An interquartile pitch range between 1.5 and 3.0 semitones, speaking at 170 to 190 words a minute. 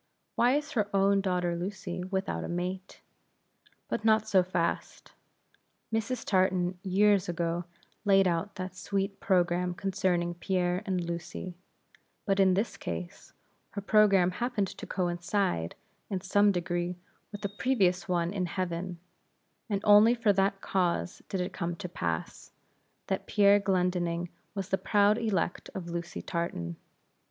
No: narrow, 2.4 semitones; average, 140 wpm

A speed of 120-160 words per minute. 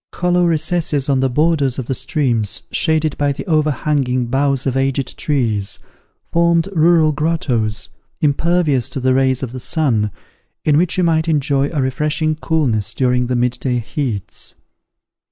Yes: average, 155 wpm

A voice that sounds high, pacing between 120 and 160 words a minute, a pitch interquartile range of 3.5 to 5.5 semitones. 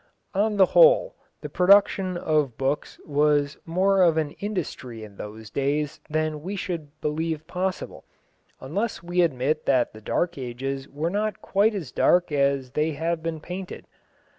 No: medium, 155 Hz; average, 155 wpm; average, 4.6 semitones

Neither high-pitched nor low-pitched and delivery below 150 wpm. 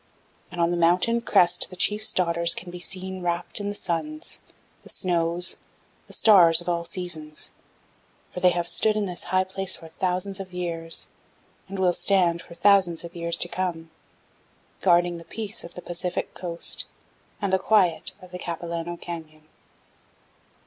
No: medium, 175 Hz; average, 165 wpm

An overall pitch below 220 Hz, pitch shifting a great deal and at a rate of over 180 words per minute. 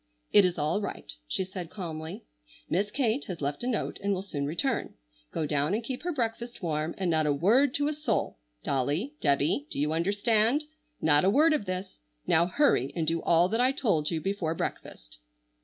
Yes: medium, 185 Hz; wide, 6.6 semitones; average, 200 wpm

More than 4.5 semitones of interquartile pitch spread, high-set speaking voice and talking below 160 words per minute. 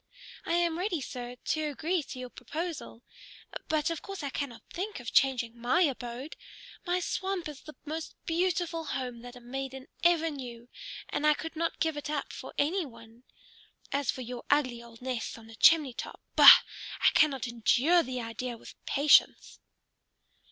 No: average, 4.9 semitones; very high, 280 Hz; average, 175 wpm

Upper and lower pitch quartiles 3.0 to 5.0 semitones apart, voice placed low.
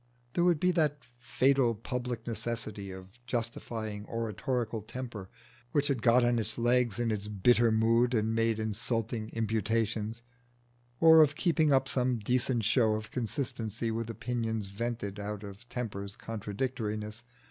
No: narrow, 2.4 semitones; low, 115 Hz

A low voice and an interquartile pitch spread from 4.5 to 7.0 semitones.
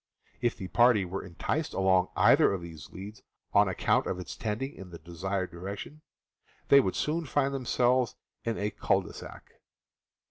Yes: low, 100 Hz; wide, 5.4 semitones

